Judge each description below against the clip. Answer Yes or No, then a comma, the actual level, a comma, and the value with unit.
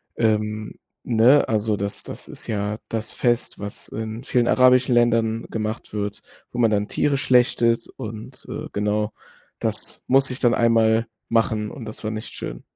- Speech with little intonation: Yes, narrow, 2.1 semitones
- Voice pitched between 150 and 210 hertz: No, low, 115 Hz